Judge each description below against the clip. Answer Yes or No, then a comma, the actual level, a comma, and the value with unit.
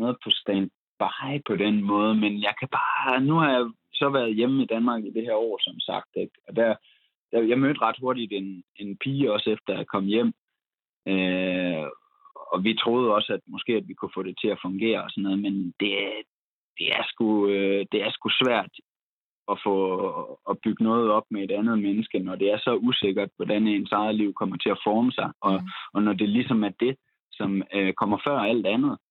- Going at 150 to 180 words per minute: No, average, 210 wpm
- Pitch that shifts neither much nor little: Yes, average, 3.5 semitones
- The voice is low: Yes, low, 105 Hz